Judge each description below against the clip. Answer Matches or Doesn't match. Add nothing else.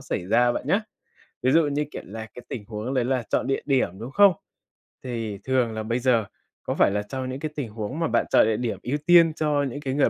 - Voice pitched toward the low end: Matches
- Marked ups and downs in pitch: Doesn't match